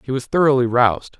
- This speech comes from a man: Yes, male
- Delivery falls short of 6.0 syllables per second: No, 6.5 syllables/s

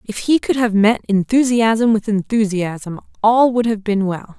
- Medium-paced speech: Yes, average, 180 wpm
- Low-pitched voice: No, high, 215 Hz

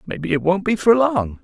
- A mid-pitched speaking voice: Yes, medium, 175 Hz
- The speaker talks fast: Yes, fast, 250 wpm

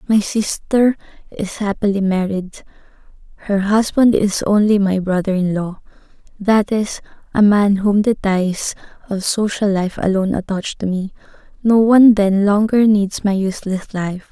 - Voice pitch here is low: No, high, 200 Hz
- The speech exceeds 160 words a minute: No, average, 145 wpm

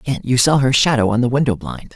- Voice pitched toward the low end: Yes, low, 125 Hz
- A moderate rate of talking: No, fast, 275 wpm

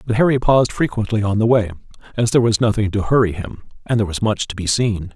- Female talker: No, male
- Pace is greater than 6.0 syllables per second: Yes, 6.8 syllables/s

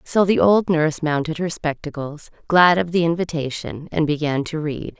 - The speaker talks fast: No, average, 180 wpm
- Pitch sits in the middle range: Yes, medium, 155 Hz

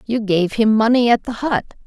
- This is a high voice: Yes, high, 225 Hz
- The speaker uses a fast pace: Yes, fast, 225 wpm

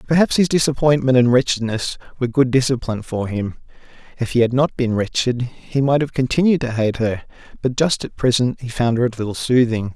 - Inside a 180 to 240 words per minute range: Yes, average, 200 wpm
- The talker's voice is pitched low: Yes, low, 125 Hz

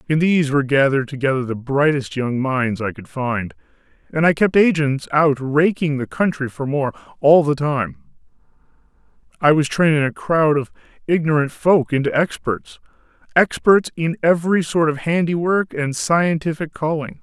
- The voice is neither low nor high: Yes, medium, 145 Hz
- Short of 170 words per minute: Yes, average, 150 wpm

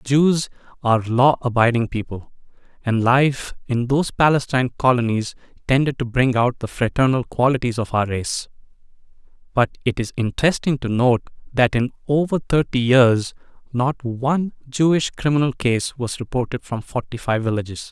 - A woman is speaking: No, male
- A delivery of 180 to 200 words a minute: No, average, 145 wpm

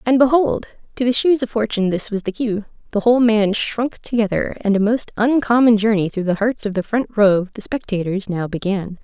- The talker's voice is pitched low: No, high, 220 Hz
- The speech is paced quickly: Yes, fast, 210 wpm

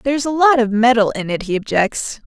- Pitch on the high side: Yes, high, 235 Hz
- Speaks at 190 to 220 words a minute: No, fast, 235 wpm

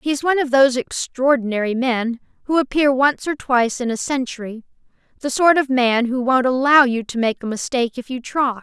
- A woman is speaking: Yes, female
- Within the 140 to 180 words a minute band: No, average, 195 wpm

